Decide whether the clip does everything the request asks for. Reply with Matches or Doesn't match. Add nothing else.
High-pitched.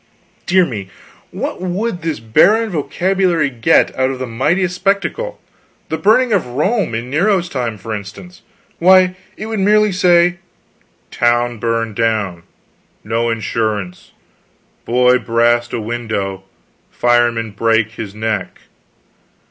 Doesn't match